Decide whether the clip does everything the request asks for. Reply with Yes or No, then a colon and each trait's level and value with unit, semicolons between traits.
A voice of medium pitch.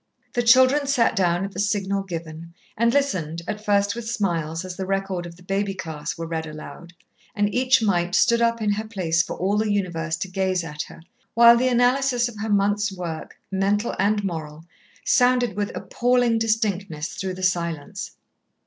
No: high, 195 Hz